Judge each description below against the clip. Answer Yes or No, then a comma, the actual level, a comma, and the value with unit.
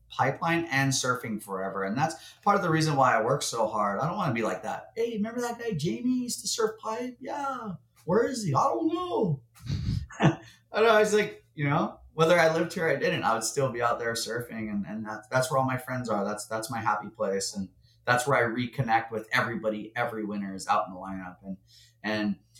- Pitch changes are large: Yes, wide, 8.8 semitones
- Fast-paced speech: Yes, fast, 230 wpm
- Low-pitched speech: Yes, low, 125 Hz